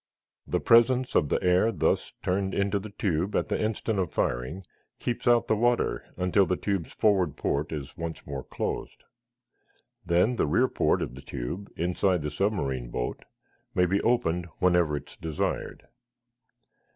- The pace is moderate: Yes, average, 165 wpm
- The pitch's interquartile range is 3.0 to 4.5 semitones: No, average, 5.0 semitones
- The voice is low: Yes, very low, 90 Hz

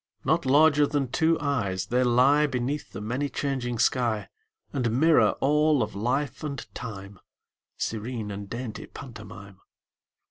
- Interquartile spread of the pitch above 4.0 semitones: Yes, average, 4.7 semitones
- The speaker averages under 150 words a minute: Yes, slow, 135 wpm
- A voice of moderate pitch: No, low, 125 Hz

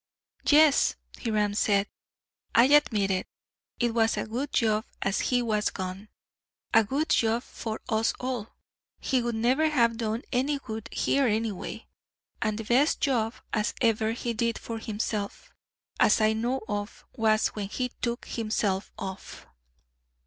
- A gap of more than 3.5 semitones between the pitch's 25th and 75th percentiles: No, narrow, 2.5 semitones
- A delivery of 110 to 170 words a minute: Yes, average, 150 wpm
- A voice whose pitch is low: No, high, 225 Hz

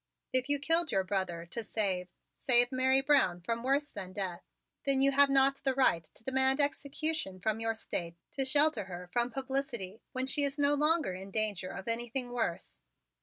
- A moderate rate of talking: Yes, average, 185 wpm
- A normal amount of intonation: No, wide, 6.1 semitones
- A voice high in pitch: Yes, very high, 250 Hz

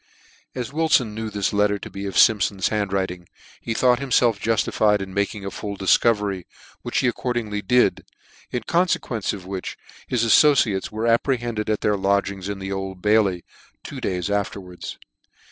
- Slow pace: No, average, 160 wpm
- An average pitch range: Yes, average, 3.0 semitones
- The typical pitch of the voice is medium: No, low, 105 Hz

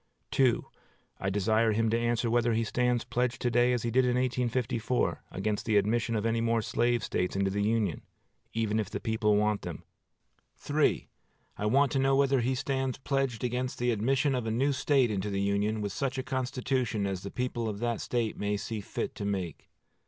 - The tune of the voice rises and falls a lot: No, average, 3.0 semitones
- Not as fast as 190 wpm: No, average, 195 wpm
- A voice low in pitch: Yes, low, 115 Hz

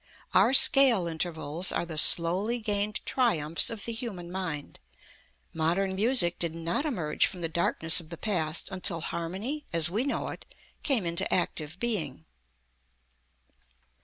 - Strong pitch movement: No, average, 4.5 semitones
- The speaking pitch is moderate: Yes, medium, 175 Hz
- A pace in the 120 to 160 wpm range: Yes, average, 140 wpm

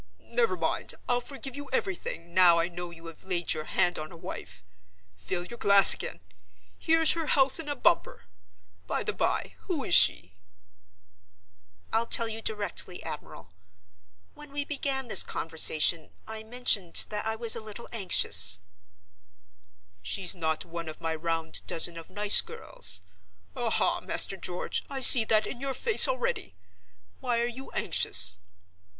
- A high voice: Yes, high, 200 Hz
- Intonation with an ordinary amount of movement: No, wide, 7.1 semitones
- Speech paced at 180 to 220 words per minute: No, average, 155 wpm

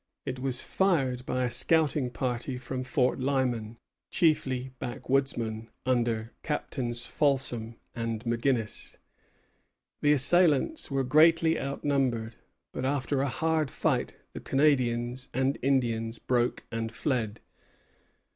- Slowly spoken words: Yes, slow, 110 wpm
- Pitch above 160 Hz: No, low, 130 Hz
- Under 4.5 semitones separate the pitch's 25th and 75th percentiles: Yes, average, 2.8 semitones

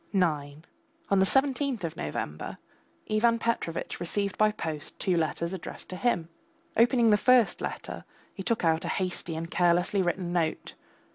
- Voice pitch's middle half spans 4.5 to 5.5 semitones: Yes, average, 4.8 semitones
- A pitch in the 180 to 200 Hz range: Yes, medium, 185 Hz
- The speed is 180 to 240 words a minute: No, average, 155 wpm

